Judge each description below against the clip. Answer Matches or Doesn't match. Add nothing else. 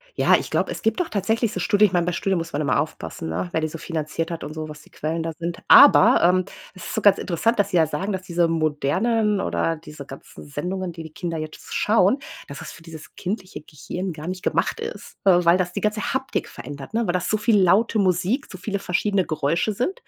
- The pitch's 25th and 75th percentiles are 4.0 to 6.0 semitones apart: Matches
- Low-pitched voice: Doesn't match